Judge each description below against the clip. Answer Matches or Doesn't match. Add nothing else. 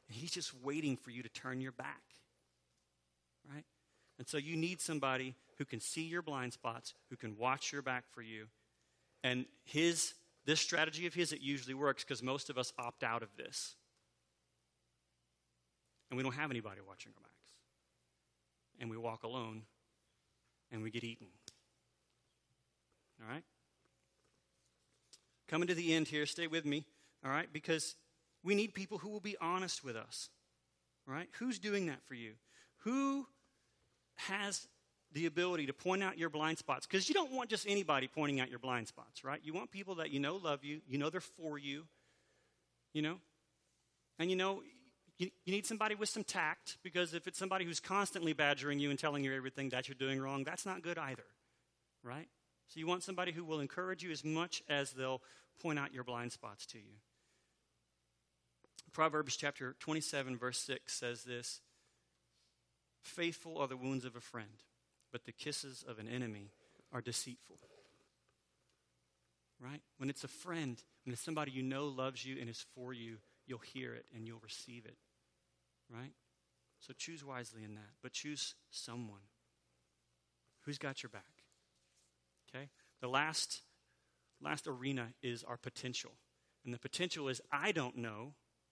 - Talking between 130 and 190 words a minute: Matches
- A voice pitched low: Matches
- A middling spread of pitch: Doesn't match